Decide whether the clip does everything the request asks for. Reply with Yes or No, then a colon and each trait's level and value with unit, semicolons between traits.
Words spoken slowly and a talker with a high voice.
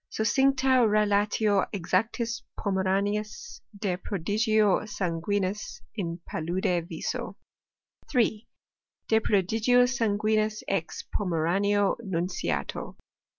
Yes: slow, 75 wpm; high, 205 Hz